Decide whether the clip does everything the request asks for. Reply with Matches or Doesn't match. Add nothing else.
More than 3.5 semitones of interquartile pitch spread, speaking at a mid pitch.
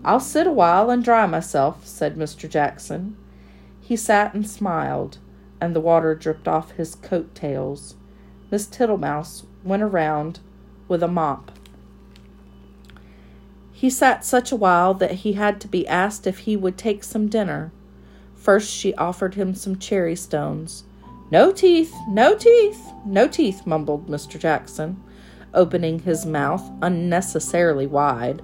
Matches